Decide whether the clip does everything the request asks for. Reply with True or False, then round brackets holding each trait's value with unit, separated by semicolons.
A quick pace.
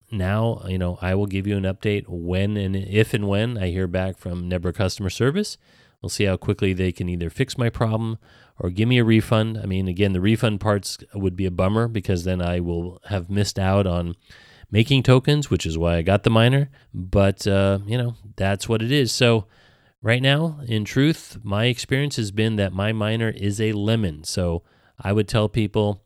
True (210 wpm)